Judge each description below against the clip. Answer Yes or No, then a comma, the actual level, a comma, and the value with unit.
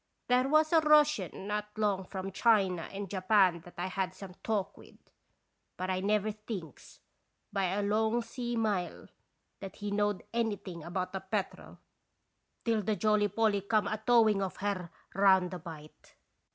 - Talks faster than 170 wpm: No, average, 165 wpm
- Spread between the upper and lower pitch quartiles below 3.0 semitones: Yes, narrow, 2.6 semitones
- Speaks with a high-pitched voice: Yes, high, 205 Hz